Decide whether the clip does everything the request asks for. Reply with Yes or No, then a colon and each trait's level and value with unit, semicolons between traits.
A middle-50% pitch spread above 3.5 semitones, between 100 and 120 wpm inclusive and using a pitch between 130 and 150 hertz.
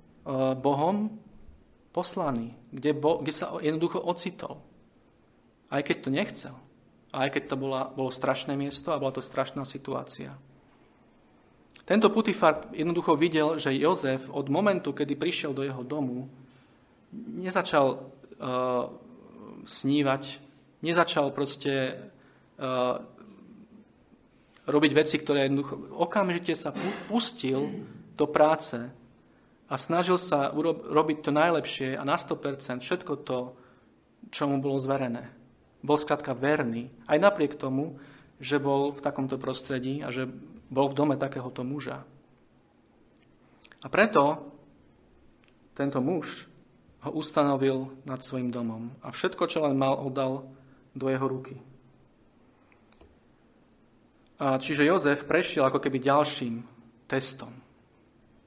No: average, 2.8 semitones; average, 115 wpm; medium, 140 Hz